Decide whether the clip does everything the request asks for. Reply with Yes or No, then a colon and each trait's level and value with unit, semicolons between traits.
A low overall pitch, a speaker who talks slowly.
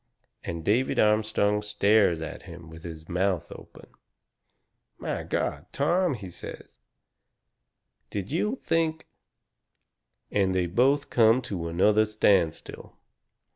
Yes: low, 105 Hz; slow, 115 wpm